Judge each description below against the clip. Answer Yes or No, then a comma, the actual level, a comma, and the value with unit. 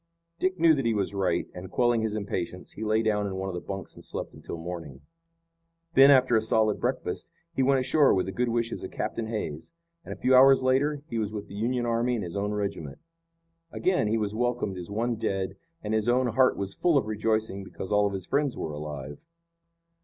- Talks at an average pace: No, fast, 220 wpm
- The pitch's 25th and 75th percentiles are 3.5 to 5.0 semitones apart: Yes, average, 4.2 semitones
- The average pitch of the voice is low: Yes, low, 110 Hz